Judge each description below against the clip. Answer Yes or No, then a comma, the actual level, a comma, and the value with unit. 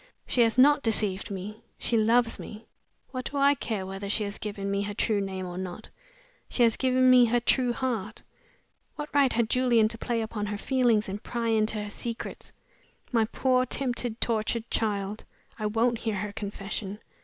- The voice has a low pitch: No, high, 225 Hz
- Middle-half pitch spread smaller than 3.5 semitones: Yes, average, 2.9 semitones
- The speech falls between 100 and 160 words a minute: No, average, 185 wpm